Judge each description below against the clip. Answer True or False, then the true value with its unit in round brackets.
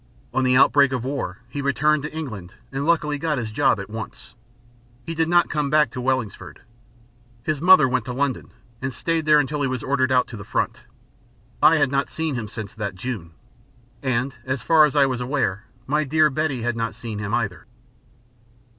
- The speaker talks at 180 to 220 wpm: True (200 wpm)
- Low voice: True (130 Hz)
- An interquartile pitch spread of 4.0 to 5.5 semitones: True (4.3 semitones)